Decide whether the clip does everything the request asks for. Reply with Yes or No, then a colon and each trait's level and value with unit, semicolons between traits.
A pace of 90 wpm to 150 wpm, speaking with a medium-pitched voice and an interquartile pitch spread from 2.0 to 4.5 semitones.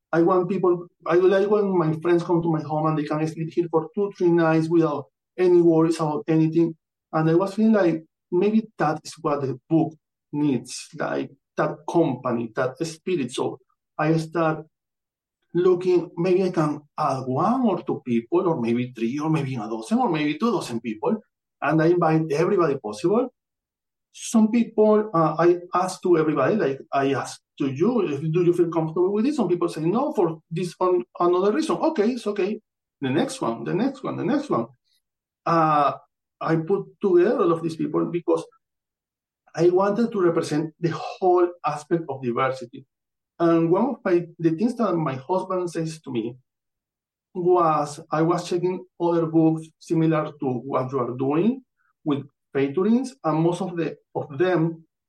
No: average, 175 wpm; medium, 165 Hz; average, 3.3 semitones